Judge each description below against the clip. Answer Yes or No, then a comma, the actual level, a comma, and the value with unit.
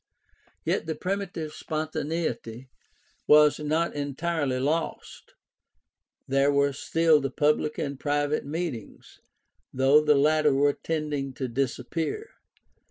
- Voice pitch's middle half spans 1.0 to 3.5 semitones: Yes, narrow, 2.4 semitones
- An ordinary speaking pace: No, slow, 110 wpm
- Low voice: No, medium, 150 Hz